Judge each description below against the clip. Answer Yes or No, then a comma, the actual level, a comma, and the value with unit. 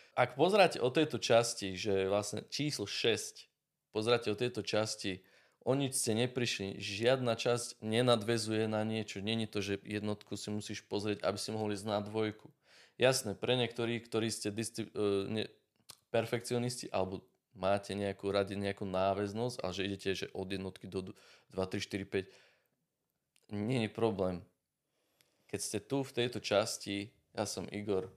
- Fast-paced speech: No, average, 155 wpm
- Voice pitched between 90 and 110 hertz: Yes, low, 105 Hz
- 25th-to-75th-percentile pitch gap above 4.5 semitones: No, average, 2.9 semitones